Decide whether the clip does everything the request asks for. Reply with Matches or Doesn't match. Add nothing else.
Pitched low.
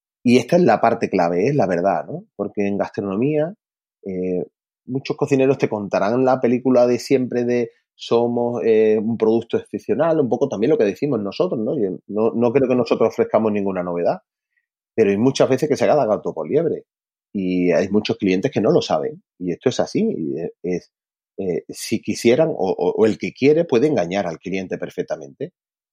Matches